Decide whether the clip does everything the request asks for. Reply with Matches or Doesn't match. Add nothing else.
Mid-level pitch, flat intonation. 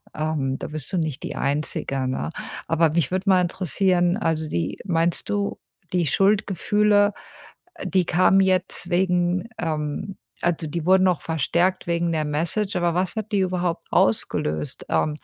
Doesn't match